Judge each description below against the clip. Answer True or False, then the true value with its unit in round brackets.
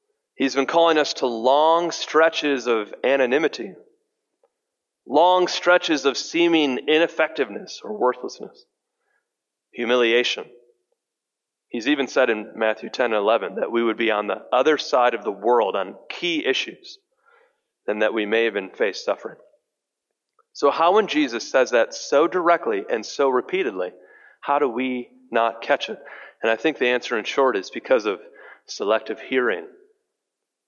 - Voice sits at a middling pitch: True (175 Hz)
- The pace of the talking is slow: False (145 wpm)